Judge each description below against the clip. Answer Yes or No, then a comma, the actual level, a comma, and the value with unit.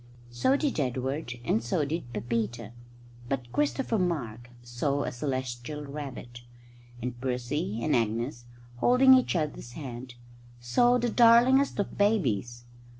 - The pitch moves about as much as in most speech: No, wide, 6.9 semitones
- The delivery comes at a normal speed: No, slow, 125 wpm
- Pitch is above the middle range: No, low, 130 Hz